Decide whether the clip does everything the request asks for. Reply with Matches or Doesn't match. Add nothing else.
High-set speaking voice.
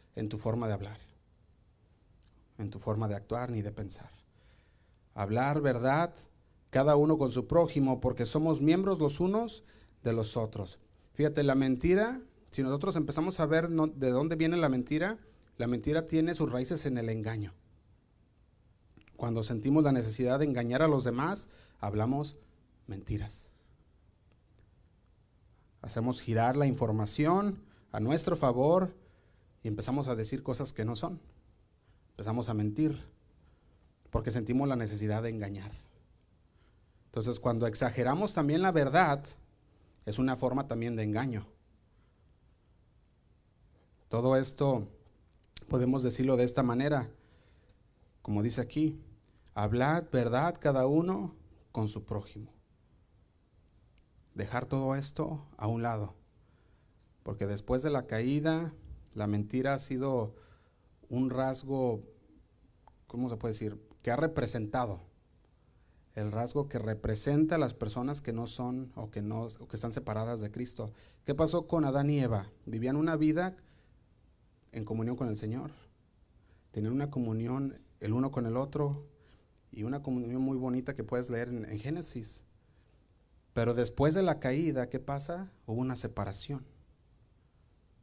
Doesn't match